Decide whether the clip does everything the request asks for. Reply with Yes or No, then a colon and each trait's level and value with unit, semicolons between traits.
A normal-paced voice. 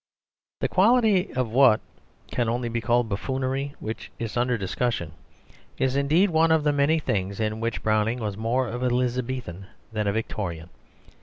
Yes: average, 165 wpm